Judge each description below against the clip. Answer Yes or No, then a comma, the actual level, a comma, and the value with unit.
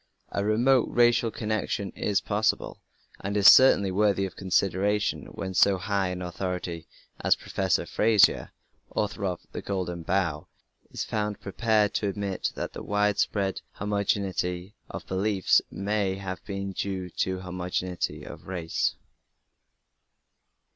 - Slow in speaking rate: Yes, slow, 125 wpm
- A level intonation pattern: Yes, narrow, 2.1 semitones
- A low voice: Yes, low, 100 Hz